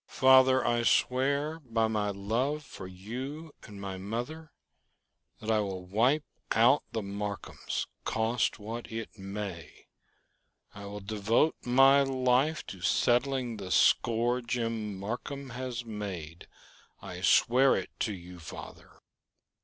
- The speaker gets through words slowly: Yes, slow, 125 wpm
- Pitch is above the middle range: No, low, 115 Hz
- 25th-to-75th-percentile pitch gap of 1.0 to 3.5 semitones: No, average, 4.3 semitones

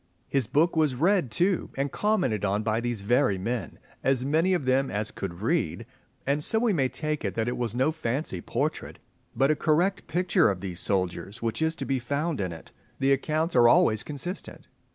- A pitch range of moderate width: No, wide, 6.3 semitones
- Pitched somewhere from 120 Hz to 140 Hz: Yes, low, 135 Hz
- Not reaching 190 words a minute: No, average, 200 wpm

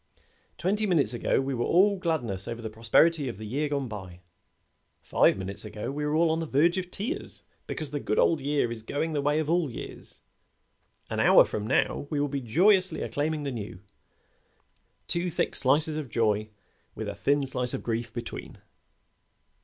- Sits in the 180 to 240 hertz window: No, medium, 145 Hz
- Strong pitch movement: Yes, wide, 5.8 semitones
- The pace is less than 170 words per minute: No, average, 185 wpm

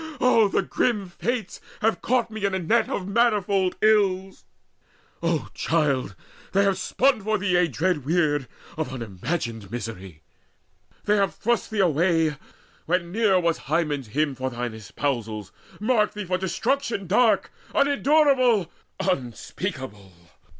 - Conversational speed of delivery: No, slow, 130 wpm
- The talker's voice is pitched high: No, medium, 180 Hz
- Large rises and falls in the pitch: Yes, wide, 6.9 semitones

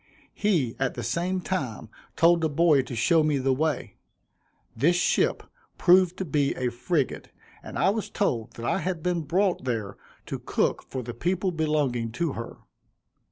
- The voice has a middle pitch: Yes, medium, 155 Hz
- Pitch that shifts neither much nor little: No, wide, 5.8 semitones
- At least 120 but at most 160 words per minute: No, average, 170 wpm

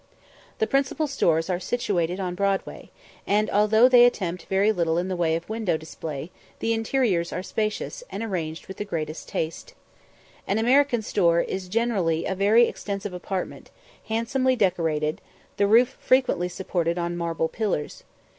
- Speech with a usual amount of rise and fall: Yes, average, 4.9 semitones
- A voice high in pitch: Yes, high, 195 Hz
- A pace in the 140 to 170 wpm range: Yes, average, 155 wpm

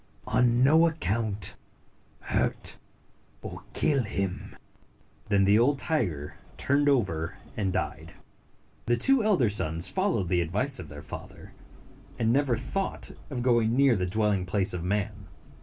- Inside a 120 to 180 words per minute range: Yes, average, 140 wpm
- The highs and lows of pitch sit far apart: Yes, wide, 6.0 semitones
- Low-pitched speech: Yes, low, 110 Hz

